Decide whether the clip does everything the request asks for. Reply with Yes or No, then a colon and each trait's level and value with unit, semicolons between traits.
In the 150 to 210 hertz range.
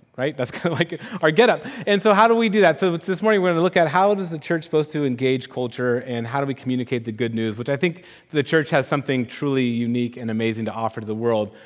No: medium, 140 Hz